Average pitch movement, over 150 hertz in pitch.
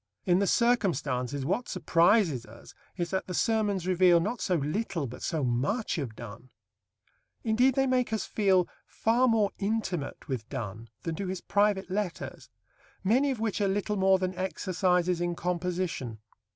Yes: average, 4.6 semitones; medium, 185 Hz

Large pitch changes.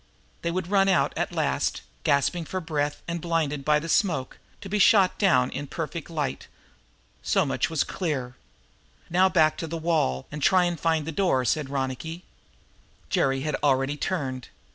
No: average, 3.8 semitones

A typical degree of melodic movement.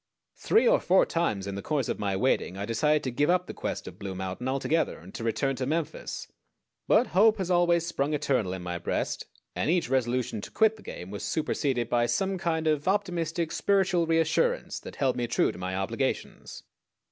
No: wide, 7.2 semitones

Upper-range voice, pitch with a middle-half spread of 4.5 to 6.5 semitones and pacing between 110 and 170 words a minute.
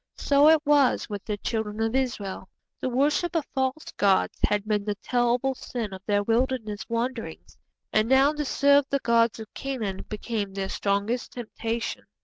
No: high, 235 Hz; average, 4.1 semitones; average, 165 wpm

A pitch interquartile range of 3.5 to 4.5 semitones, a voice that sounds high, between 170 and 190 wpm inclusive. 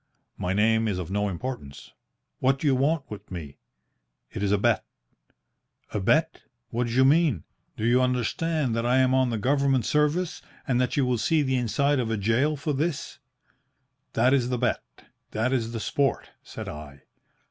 No: average, 3.8 semitones; low, 125 Hz; average, 180 wpm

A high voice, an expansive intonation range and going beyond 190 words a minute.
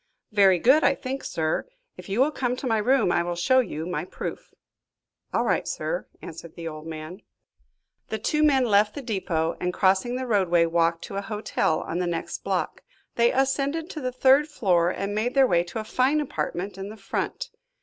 Yes: high, 210 Hz; wide, 6.8 semitones; average, 200 wpm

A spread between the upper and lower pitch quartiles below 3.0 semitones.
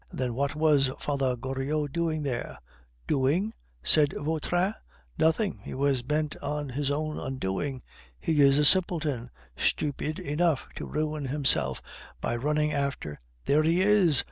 Yes: narrow, 2.6 semitones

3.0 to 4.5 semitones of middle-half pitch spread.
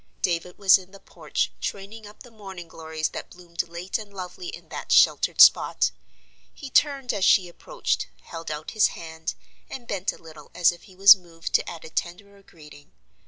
Yes: average, 3.4 semitones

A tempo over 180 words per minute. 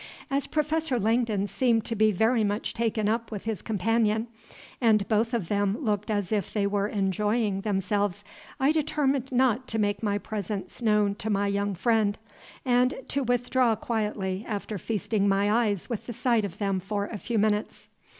No: average, 175 wpm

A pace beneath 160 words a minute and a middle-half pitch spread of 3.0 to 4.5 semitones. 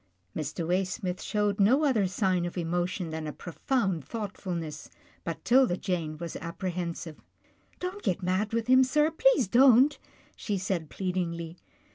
No: average, 145 wpm; average, 5.2 semitones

